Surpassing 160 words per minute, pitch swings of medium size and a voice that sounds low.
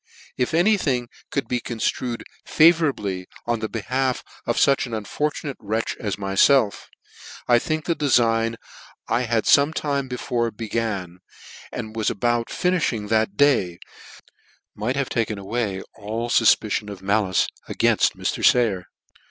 No: average, 140 wpm; average, 4.1 semitones; low, 115 Hz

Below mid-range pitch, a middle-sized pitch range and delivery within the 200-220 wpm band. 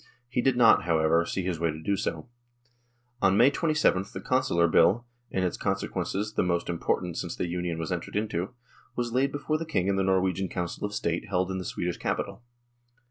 Yes: very low, 95 Hz; average, 4.3 semitones; fast, 205 wpm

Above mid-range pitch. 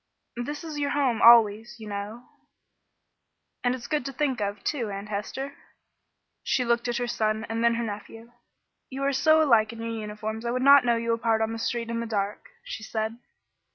Yes: high, 230 Hz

